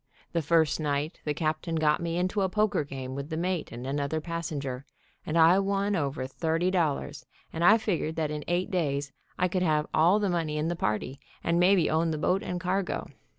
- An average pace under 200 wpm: No, fast, 205 wpm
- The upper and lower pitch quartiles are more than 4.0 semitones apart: No, average, 3.2 semitones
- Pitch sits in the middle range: Yes, medium, 165 Hz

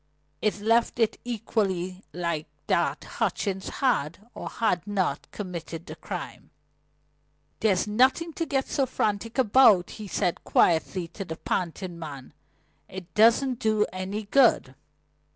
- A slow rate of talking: Yes, slow, 130 wpm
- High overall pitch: Yes, high, 205 Hz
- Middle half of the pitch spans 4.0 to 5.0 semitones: Yes, average, 4.4 semitones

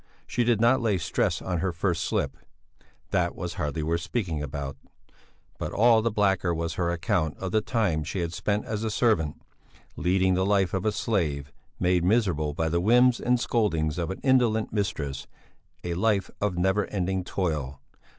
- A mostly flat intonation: No, average, 4.5 semitones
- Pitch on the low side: Yes, very low, 95 Hz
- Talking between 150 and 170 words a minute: No, average, 180 wpm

